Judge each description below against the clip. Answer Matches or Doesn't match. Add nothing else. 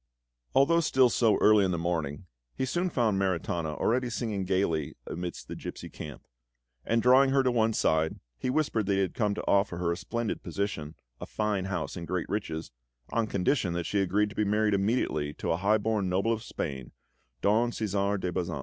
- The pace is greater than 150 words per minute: Matches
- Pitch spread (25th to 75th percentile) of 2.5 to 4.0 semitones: Doesn't match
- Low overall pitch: Matches